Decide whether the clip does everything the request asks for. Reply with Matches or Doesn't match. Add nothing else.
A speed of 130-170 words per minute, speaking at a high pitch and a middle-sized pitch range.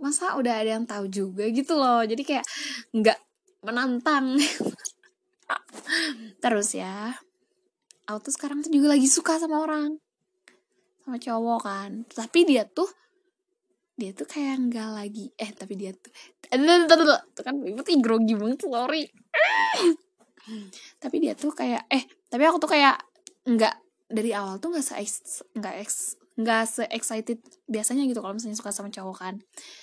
Doesn't match